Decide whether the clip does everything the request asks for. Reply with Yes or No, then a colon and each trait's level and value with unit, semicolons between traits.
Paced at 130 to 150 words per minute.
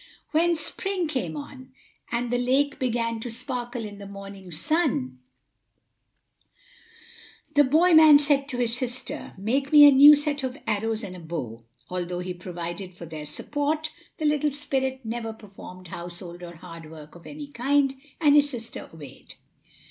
No: average, 160 wpm